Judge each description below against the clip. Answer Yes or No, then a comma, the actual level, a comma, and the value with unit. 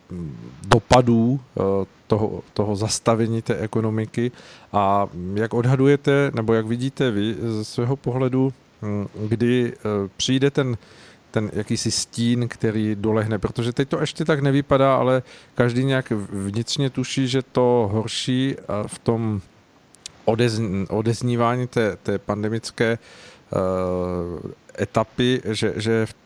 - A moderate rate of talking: No, slow, 110 wpm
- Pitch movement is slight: No, average, 3.2 semitones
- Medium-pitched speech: No, low, 115 Hz